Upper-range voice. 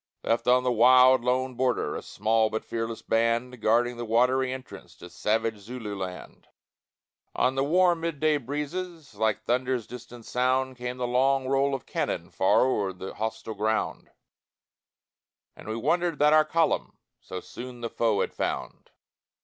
No: low, 125 Hz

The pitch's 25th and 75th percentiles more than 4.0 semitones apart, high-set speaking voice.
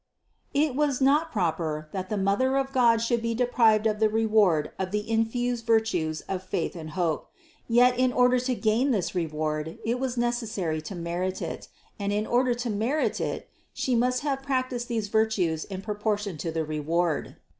Yes: wide, 5.5 semitones; high, 220 Hz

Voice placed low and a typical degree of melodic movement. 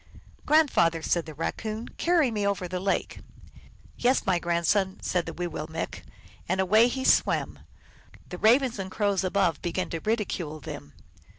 No: high, 190 Hz; average, 4.3 semitones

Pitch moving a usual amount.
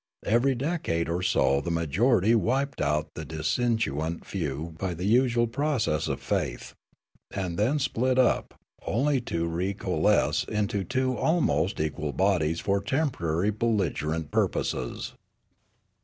No: wide, 7.1 semitones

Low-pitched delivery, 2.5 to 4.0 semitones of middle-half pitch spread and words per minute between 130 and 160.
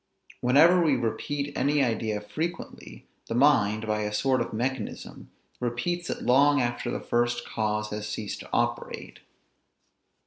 No: low, 120 Hz; average, 4.8 semitones; average, 140 wpm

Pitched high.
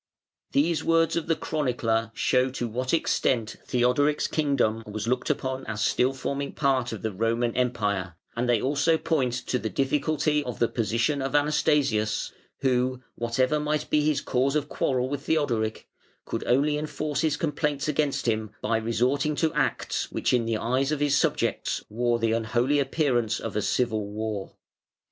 No: low, 130 Hz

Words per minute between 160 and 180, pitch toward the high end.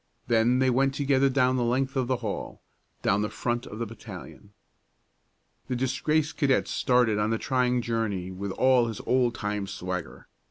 No: average, 175 wpm; low, 120 Hz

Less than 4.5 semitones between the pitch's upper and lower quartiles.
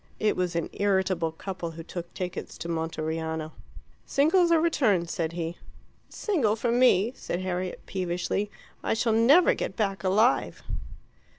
No: average, 5.2 semitones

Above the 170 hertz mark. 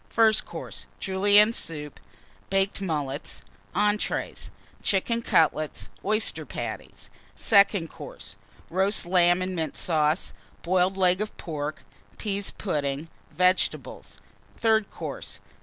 Yes: medium, 185 Hz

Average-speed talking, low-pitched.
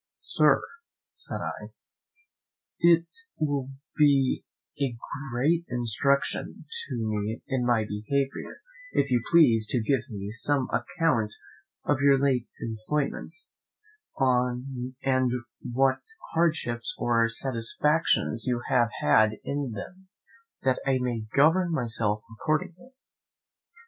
No: slow, 105 wpm; low, 130 Hz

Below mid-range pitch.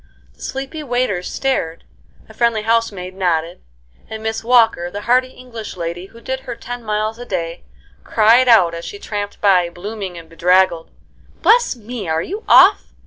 No: high, 215 Hz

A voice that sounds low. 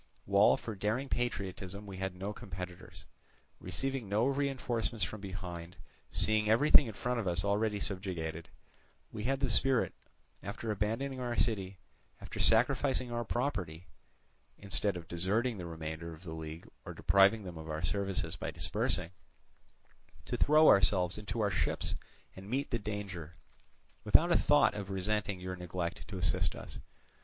Yes: low, 100 Hz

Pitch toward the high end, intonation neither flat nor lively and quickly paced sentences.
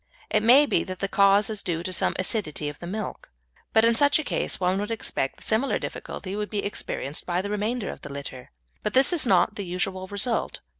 Yes: high, 200 Hz; average, 3.4 semitones; fast, 230 wpm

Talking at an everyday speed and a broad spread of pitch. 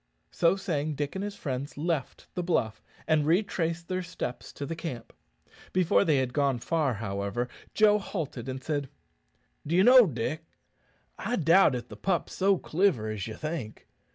Yes: average, 165 wpm; wide, 6.0 semitones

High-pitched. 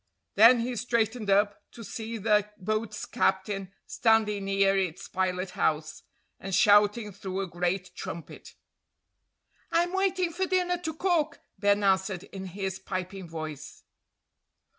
Yes: high, 205 Hz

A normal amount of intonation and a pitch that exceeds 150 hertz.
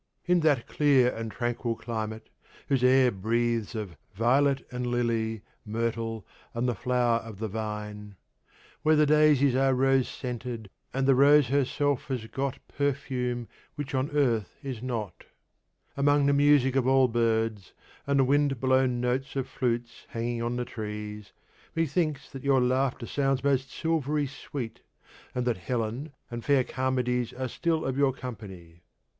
No: average, 3.2 semitones; low, 125 Hz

